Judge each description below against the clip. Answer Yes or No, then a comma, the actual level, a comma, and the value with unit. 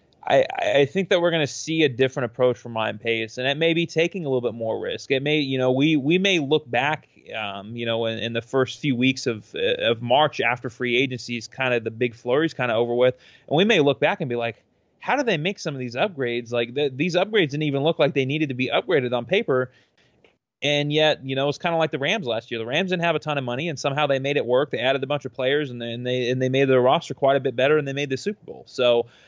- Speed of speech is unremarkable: No, fast, 285 wpm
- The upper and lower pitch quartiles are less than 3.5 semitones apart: No, average, 3.8 semitones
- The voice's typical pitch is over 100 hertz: Yes, low, 135 Hz